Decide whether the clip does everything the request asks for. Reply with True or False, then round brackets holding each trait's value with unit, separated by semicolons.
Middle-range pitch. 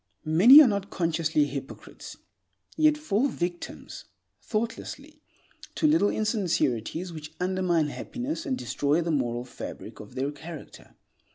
True (175 Hz)